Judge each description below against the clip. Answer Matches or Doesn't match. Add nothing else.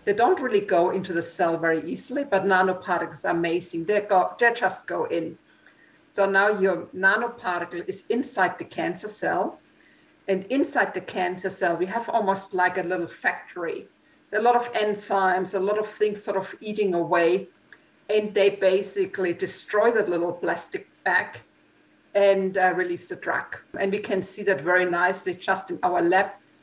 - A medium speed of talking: Matches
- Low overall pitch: Doesn't match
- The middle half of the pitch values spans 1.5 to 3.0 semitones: Matches